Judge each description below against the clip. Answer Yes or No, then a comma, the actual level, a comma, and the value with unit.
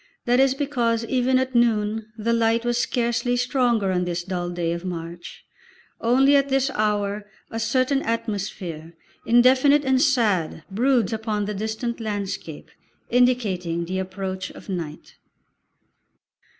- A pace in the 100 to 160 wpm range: Yes, slow, 135 wpm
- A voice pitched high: Yes, high, 225 Hz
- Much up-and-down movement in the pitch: No, average, 4.7 semitones